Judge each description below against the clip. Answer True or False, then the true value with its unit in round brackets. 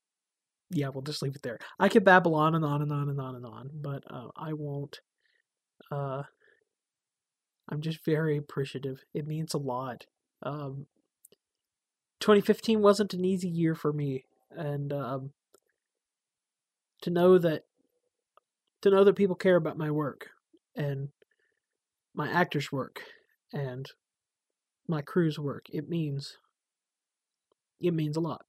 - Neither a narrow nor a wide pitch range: False (5.9 semitones)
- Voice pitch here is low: False (155 Hz)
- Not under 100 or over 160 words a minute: True (140 wpm)